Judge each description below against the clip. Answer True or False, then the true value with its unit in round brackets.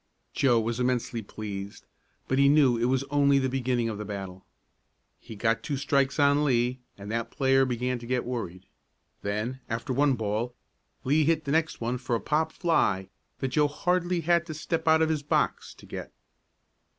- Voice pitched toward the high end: False (130 Hz)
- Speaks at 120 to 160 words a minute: False (185 wpm)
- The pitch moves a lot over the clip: False (4.2 semitones)